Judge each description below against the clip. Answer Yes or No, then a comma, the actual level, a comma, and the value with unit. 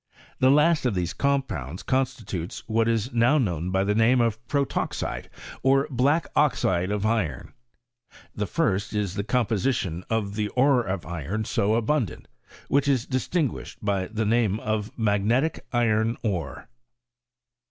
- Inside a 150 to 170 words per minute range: No, average, 140 wpm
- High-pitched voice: No, low, 110 Hz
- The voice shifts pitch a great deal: No, average, 4.5 semitones